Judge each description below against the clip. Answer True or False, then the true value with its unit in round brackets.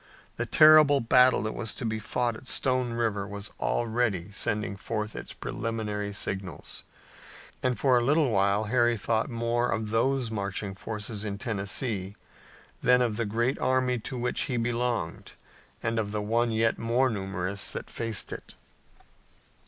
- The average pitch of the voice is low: True (115 Hz)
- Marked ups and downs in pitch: False (2.9 semitones)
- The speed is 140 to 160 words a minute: True (155 wpm)